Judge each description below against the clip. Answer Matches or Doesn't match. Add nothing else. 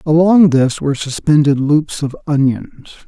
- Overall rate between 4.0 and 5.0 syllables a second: Matches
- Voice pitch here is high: Doesn't match